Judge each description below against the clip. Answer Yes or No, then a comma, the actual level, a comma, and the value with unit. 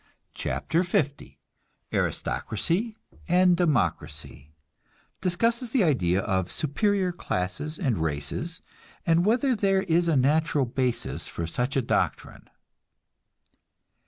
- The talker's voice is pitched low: No, medium, 160 Hz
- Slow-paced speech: Yes, slow, 100 wpm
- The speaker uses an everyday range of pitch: No, wide, 8.3 semitones